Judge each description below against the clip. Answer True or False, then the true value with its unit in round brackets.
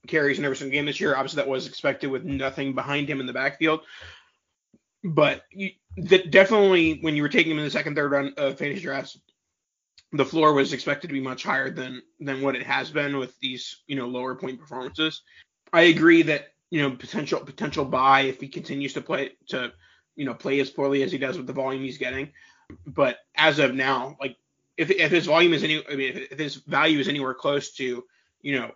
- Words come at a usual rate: False (220 wpm)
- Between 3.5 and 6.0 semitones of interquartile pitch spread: False (2.7 semitones)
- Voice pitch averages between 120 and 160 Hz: True (140 Hz)